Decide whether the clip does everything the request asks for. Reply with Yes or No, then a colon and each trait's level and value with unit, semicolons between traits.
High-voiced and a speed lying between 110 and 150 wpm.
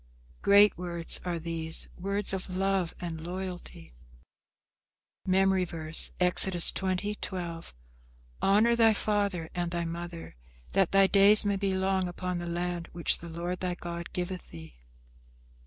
No: medium, 180 Hz; average, 140 wpm